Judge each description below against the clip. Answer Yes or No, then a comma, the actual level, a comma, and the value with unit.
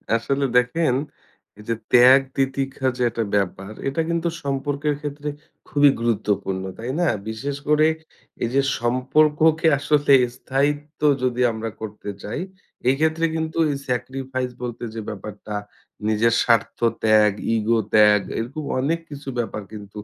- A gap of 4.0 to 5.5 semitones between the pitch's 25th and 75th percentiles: Yes, average, 4.6 semitones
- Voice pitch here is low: Yes, low, 130 Hz